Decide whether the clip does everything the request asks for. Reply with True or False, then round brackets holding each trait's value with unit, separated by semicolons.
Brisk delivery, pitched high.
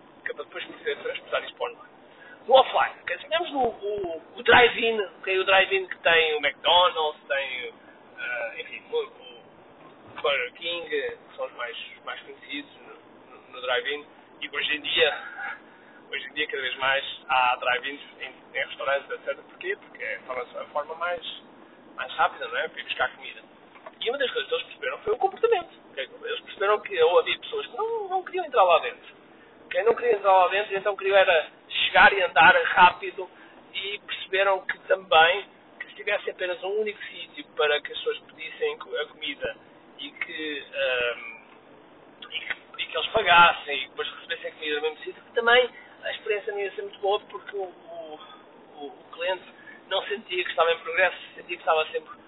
True (190 wpm; 290 Hz)